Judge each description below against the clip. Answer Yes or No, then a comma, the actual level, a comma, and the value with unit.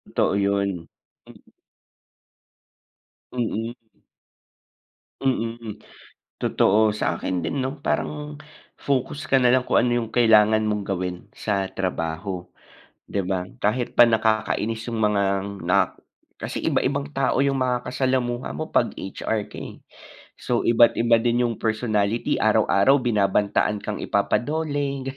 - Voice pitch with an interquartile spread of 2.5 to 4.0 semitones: Yes, average, 3.7 semitones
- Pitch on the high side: No, low, 110 Hz